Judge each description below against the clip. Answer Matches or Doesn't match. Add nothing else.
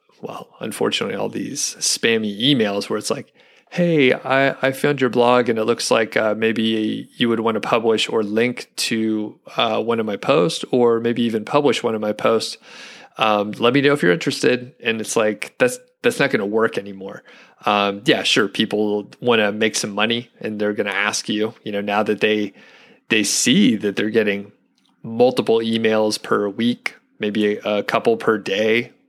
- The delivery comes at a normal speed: Matches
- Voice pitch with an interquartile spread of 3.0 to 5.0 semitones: Matches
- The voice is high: Doesn't match